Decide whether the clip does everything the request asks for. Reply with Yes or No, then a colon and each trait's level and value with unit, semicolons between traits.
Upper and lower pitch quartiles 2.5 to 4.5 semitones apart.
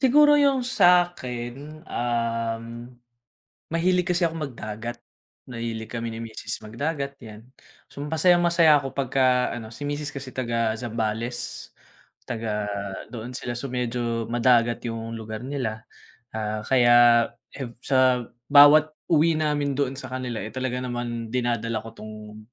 Yes: average, 3.7 semitones